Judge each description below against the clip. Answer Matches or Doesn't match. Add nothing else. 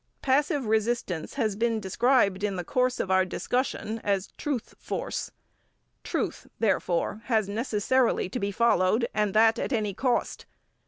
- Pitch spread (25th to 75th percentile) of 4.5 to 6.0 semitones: Doesn't match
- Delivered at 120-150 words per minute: Matches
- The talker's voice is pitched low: Doesn't match